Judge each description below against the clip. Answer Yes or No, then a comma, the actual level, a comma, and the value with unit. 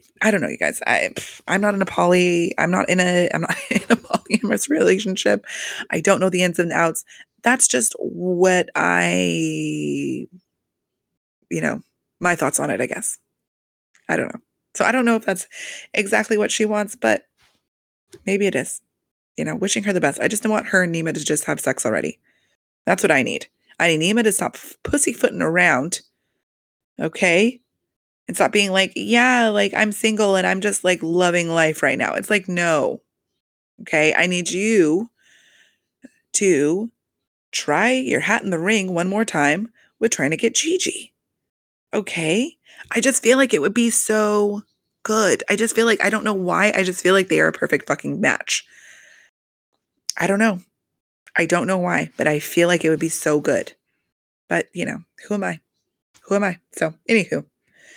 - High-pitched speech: Yes, high, 195 Hz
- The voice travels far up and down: No, average, 4.2 semitones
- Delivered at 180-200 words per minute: Yes, average, 185 wpm